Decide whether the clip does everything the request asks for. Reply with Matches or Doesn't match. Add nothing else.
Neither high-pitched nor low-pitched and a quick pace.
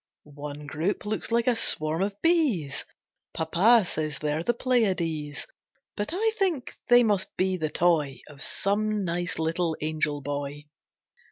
Doesn't match